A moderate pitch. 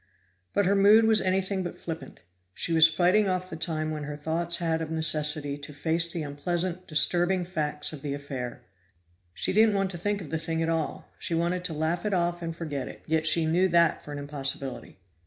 Yes: medium, 165 Hz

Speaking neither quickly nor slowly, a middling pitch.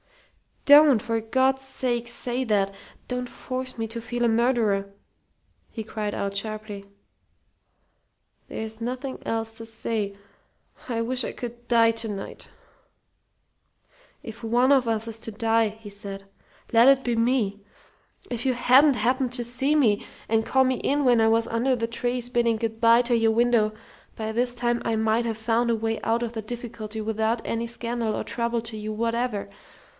No: average, 170 wpm; high, 230 Hz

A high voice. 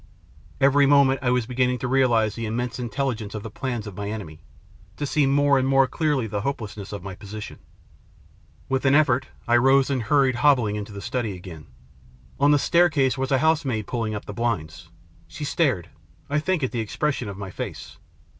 No: low, 125 Hz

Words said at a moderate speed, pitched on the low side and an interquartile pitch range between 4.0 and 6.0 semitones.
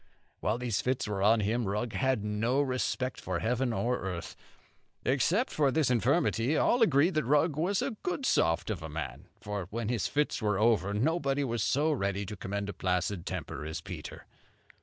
Yes: average, 180 wpm; low, 115 Hz; wide, 5.5 semitones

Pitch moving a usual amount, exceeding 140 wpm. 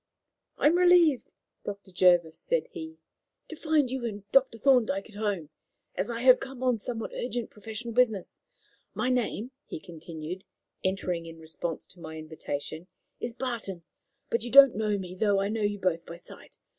No: wide, 5.8 semitones; average, 170 wpm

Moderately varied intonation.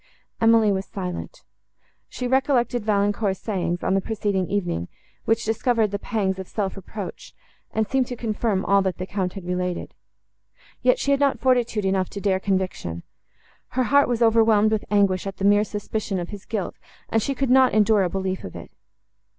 Yes: average, 3.1 semitones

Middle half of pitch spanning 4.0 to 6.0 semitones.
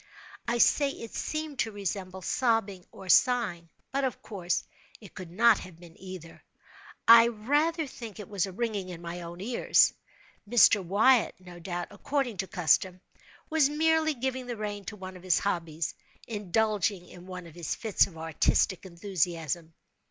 Yes: average, 5.0 semitones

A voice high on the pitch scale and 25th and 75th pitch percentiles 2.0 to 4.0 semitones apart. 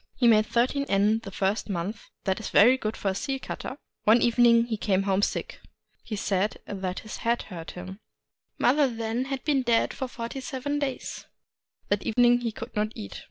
Yes: high, 225 Hz; average, 3.7 semitones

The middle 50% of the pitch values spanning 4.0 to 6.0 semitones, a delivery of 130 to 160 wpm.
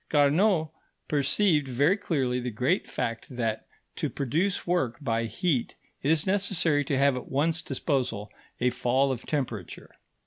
Yes: average, 4.6 semitones; average, 145 wpm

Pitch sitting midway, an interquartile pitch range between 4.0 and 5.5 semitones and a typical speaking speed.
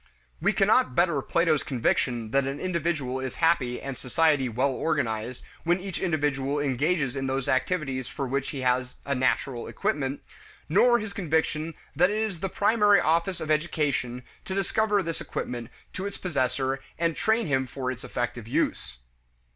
Yes: medium, 145 Hz; average, 4.9 semitones; average, 165 wpm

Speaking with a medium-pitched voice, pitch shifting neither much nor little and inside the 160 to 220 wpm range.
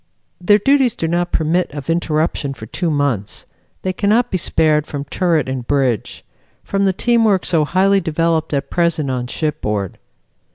Yes: medium, 160 Hz; average, 4.7 semitones; average, 165 wpm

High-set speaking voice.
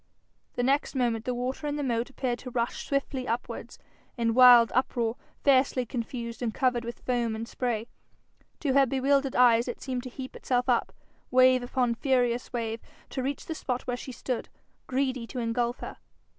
Yes: very high, 250 Hz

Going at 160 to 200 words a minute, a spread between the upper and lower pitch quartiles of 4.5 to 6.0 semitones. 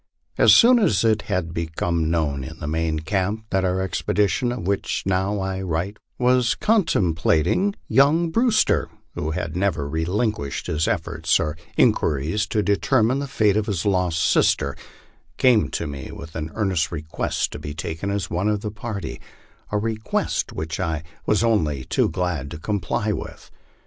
Yes: average, 170 wpm; average, 5.1 semitones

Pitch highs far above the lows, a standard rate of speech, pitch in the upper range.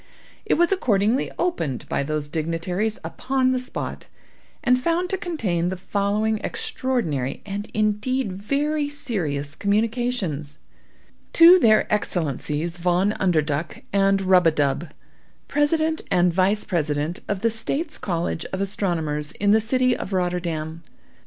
No: wide, 7.0 semitones; slow, 130 wpm; high, 200 Hz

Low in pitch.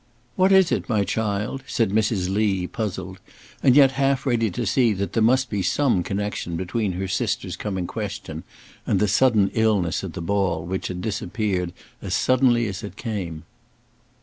Yes: low, 105 Hz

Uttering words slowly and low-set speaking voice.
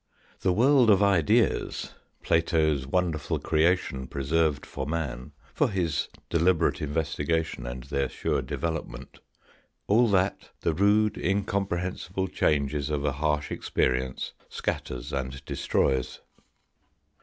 Yes: slow, 110 wpm; very low, 80 Hz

